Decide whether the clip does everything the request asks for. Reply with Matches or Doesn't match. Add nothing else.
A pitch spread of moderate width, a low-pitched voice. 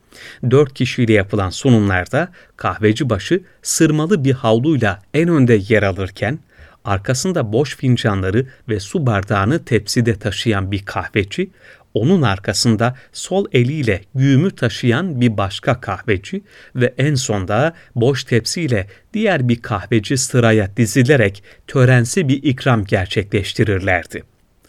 Matches